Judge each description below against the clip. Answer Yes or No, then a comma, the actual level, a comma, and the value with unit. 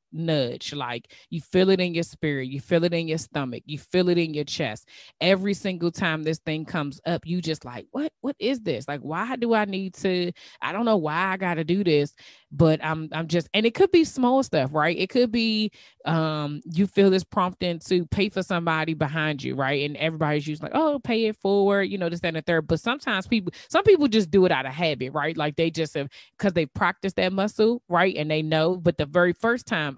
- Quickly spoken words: Yes, fast, 240 wpm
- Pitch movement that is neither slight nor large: Yes, average, 4.2 semitones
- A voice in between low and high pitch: Yes, medium, 170 Hz